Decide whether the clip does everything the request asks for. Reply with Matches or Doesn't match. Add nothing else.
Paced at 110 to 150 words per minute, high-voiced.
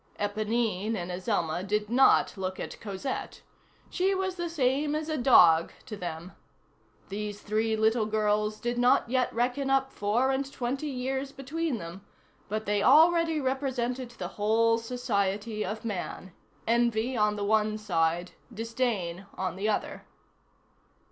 Matches